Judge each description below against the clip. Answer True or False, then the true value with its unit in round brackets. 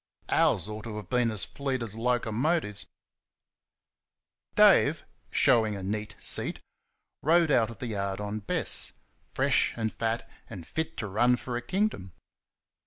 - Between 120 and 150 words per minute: True (140 wpm)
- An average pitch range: True (3.2 semitones)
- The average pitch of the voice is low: True (115 Hz)